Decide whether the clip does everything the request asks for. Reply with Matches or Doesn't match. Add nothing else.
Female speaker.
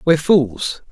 Doesn't match